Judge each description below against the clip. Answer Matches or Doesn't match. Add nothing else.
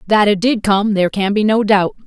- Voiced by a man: Doesn't match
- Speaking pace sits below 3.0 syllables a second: Doesn't match